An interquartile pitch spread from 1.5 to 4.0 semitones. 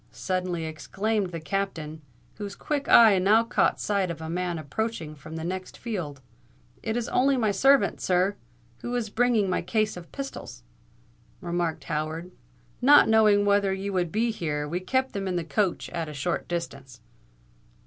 No: average, 4.8 semitones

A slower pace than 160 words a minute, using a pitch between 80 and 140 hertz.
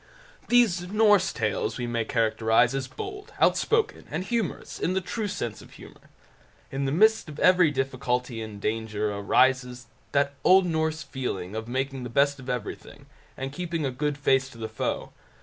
No: average, 175 wpm; low, 135 Hz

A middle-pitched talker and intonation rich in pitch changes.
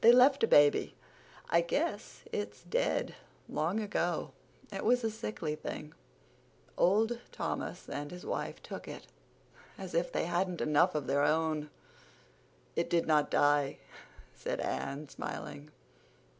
Yes: medium, 170 Hz; wide, 6.6 semitones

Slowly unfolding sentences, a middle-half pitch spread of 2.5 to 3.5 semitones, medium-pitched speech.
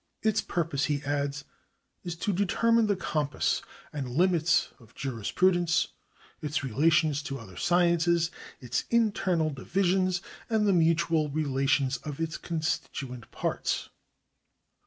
No: slow, 130 wpm; average, 4.0 semitones; medium, 160 Hz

